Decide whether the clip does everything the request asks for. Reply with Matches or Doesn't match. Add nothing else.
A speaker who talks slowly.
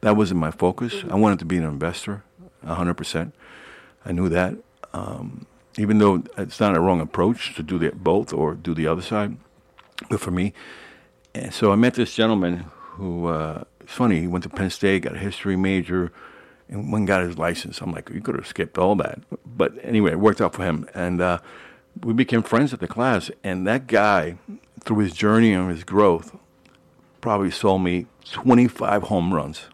Doesn't match